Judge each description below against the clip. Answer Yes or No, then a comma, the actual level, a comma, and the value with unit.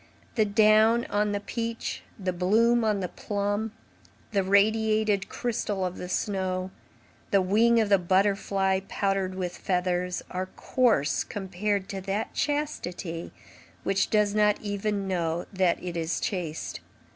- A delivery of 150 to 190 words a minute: No, slow, 135 wpm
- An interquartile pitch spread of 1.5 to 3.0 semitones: Yes, narrow, 2.6 semitones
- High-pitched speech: Yes, high, 200 Hz